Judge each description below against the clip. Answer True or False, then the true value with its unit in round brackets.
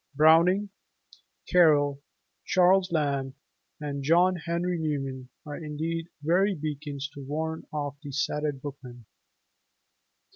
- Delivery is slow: True (105 wpm)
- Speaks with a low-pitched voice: False (150 Hz)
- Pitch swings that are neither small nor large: True (3.0 semitones)